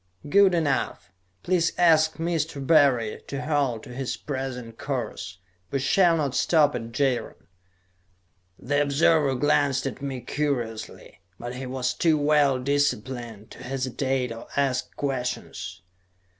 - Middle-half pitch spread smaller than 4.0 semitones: Yes, average, 2.9 semitones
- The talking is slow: Yes, slow, 130 wpm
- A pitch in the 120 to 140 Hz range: Yes, low, 135 Hz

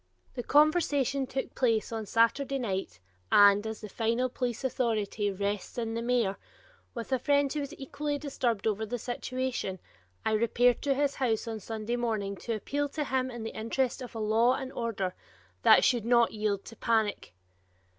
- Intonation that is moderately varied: Yes, average, 3.3 semitones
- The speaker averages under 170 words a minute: No, average, 175 wpm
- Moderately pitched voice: No, high, 235 Hz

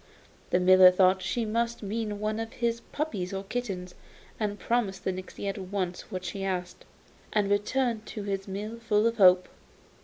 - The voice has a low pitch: No, high, 205 Hz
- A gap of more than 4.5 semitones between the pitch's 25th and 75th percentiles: No, average, 3.2 semitones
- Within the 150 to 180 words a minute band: Yes, average, 175 wpm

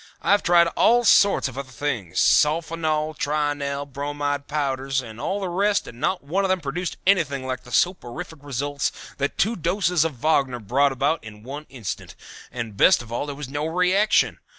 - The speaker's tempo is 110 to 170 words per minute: No, average, 185 wpm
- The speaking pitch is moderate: Yes, medium, 145 Hz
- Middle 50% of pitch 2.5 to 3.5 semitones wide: No, average, 4.4 semitones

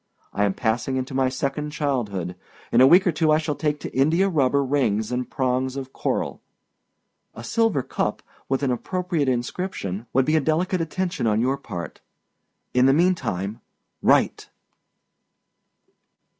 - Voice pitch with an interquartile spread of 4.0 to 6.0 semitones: Yes, average, 4.3 semitones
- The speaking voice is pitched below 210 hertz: Yes, low, 135 Hz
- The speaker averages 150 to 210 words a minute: Yes, average, 155 wpm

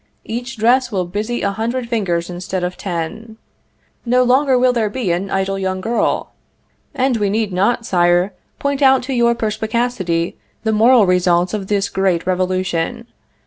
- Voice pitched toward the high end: Yes, high, 210 Hz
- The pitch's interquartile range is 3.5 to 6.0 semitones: Yes, average, 4.6 semitones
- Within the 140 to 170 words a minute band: Yes, average, 160 wpm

